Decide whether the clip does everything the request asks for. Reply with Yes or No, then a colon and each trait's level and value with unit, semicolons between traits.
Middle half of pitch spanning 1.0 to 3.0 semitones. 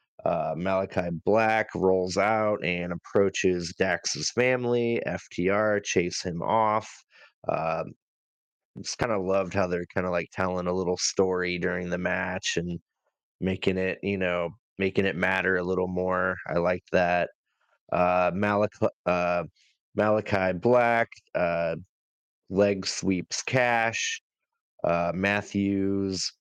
Yes: average, 2.7 semitones